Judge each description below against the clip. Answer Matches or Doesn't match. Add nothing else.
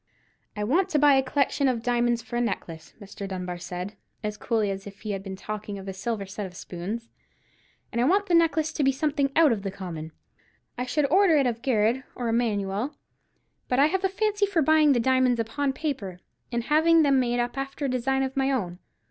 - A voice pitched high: Matches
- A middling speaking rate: Doesn't match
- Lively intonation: Matches